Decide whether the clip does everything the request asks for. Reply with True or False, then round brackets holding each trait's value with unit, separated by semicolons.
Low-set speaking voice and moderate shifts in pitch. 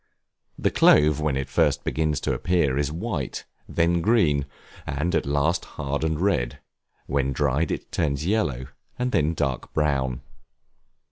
True (75 Hz; 3.3 semitones)